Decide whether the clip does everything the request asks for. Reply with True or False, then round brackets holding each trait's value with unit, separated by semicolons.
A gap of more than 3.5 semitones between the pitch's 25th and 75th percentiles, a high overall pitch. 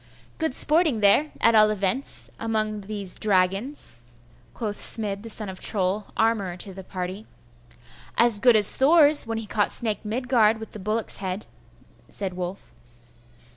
False (2.7 semitones; 215 Hz)